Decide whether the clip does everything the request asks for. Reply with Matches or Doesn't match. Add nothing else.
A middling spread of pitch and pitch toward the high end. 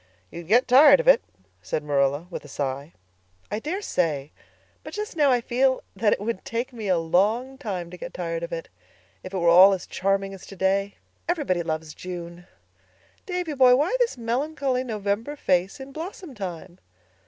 Doesn't match